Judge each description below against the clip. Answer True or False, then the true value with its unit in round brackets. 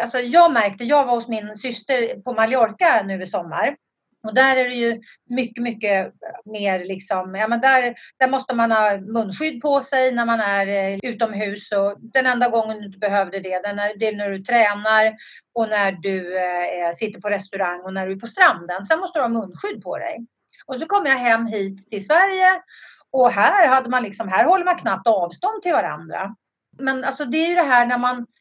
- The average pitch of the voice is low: False (230 Hz)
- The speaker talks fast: True (205 wpm)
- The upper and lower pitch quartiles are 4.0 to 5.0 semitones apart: True (4.3 semitones)